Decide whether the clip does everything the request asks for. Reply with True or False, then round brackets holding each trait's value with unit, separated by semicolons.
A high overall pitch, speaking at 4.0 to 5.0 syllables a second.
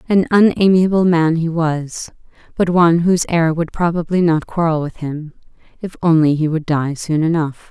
False (165 Hz; 4.9 syllables/s)